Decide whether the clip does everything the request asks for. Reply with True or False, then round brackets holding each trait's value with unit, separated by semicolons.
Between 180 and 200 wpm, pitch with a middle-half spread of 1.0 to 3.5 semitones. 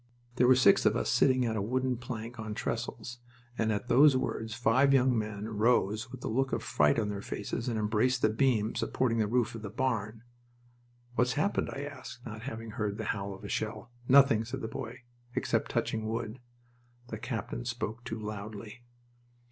True (190 wpm; 2.8 semitones)